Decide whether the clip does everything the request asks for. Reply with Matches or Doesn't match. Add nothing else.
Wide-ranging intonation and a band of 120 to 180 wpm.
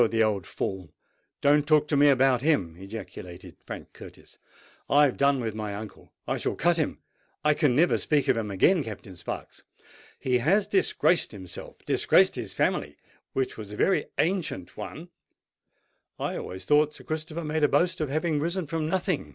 Matches